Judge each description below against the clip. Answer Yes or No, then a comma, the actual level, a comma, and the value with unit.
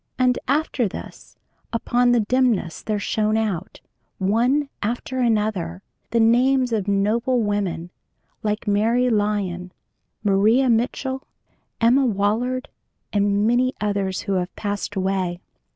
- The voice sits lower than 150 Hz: No, high, 215 Hz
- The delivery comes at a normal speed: No, slow, 120 wpm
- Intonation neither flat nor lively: Yes, average, 3.4 semitones